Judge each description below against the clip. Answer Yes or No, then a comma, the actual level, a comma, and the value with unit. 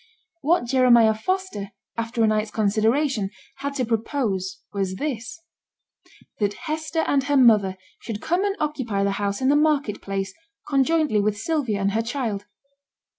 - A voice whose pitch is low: No, high, 230 Hz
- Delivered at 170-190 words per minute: No, average, 150 wpm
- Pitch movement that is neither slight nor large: No, wide, 5.8 semitones